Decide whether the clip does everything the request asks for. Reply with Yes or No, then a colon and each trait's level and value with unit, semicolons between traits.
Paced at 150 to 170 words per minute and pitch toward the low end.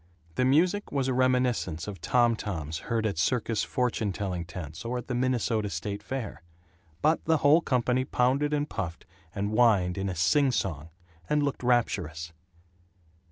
Yes: average, 160 wpm; low, 115 Hz